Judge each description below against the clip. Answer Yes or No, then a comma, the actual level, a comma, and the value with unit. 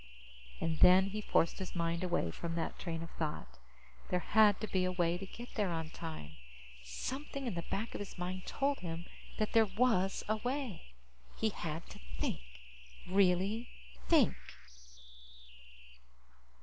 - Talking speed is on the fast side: No, average, 155 wpm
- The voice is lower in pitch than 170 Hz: No, medium, 185 Hz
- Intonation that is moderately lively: Yes, average, 4.4 semitones